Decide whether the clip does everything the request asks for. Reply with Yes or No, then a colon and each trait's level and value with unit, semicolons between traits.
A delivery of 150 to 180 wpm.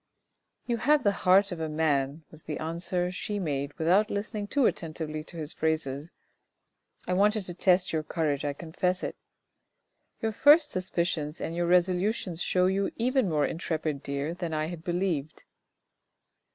Yes: average, 165 wpm